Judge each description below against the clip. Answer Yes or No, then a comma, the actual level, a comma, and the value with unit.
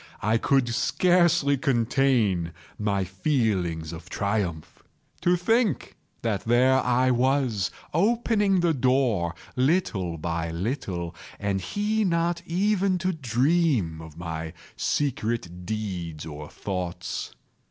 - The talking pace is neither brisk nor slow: No, slow, 110 wpm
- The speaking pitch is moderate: No, low, 115 Hz